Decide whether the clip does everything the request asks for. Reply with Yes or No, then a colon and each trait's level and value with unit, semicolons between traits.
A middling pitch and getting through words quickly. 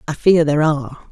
Yes: medium, 155 Hz; fast, 215 wpm